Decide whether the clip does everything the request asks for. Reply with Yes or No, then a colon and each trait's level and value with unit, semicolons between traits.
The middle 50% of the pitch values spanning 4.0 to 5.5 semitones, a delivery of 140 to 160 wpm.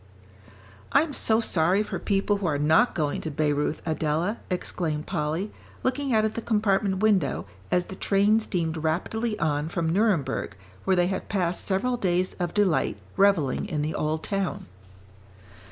Yes: average, 4.7 semitones; average, 155 wpm